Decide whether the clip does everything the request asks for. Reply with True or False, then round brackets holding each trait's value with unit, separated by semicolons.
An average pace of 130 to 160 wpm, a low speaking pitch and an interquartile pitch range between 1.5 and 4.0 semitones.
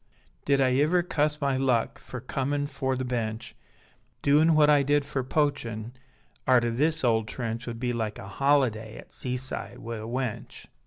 False (170 wpm; 130 Hz; 3.6 semitones)